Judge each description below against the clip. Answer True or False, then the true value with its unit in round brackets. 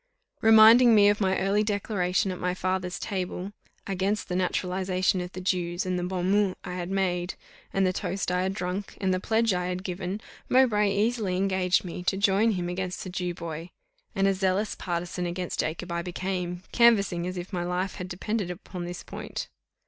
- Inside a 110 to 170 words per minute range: False (195 wpm)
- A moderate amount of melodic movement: False (1.8 semitones)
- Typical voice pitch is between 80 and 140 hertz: False (185 Hz)